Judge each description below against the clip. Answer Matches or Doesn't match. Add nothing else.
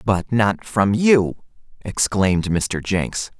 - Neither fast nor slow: Doesn't match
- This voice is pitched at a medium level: Doesn't match